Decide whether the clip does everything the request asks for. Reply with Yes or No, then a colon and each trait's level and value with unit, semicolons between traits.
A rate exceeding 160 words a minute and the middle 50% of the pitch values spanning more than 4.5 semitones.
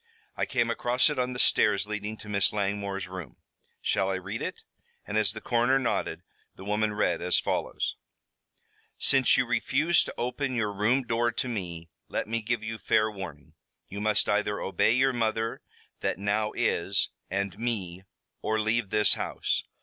No: average, 170 wpm; average, 3.1 semitones